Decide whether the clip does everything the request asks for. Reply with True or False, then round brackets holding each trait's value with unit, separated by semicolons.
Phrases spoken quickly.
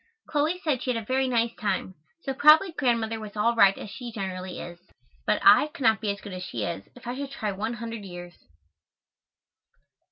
True (210 wpm)